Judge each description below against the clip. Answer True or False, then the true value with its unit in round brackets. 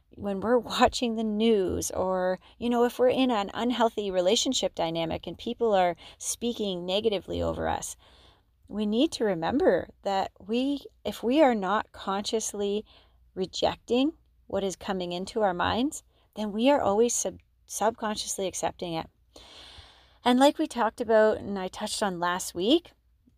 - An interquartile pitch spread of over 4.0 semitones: True (4.5 semitones)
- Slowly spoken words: False (150 wpm)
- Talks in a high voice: True (210 Hz)